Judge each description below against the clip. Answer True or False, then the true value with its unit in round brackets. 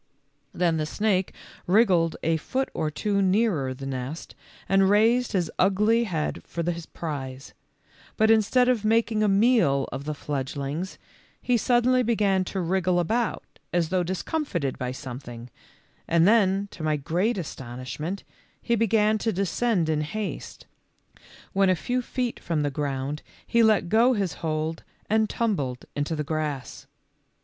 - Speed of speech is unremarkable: True (150 wpm)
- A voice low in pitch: False (185 Hz)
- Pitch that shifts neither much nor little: False (6.2 semitones)